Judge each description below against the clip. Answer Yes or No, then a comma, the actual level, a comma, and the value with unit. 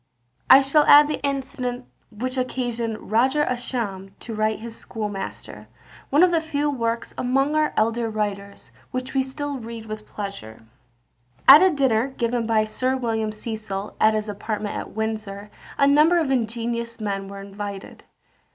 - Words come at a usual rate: Yes, average, 155 wpm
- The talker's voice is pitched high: Yes, high, 230 Hz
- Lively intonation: No, average, 3.8 semitones